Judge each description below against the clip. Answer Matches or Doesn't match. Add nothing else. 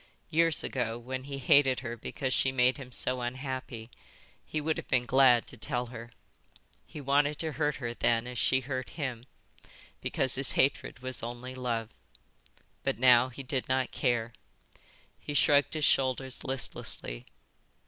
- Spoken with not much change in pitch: Matches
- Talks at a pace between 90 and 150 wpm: Doesn't match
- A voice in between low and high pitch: Doesn't match